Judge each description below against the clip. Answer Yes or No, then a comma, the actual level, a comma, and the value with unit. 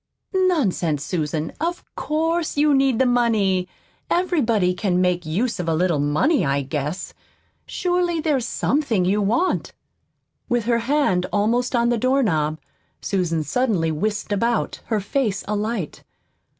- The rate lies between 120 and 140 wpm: Yes, slow, 135 wpm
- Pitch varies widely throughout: Yes, wide, 7.0 semitones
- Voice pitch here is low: No, high, 215 Hz